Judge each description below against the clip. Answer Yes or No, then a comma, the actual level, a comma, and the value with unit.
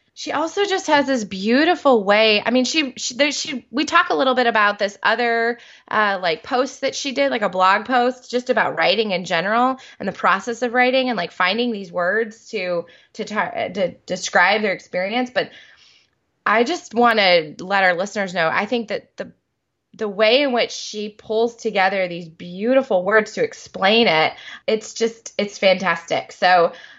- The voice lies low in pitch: No, high, 230 Hz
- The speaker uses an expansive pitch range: No, average, 4.4 semitones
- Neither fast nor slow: Yes, average, 185 wpm